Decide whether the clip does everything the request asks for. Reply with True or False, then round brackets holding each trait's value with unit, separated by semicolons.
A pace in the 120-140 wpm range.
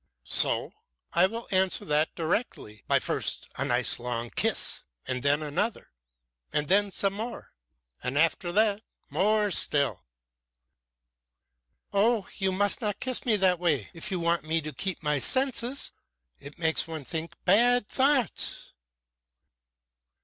True (135 wpm)